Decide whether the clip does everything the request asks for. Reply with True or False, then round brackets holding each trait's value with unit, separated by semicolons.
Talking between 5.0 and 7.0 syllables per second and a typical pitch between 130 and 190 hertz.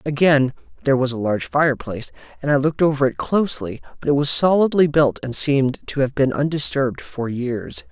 True (6.0 syllables/s; 140 Hz)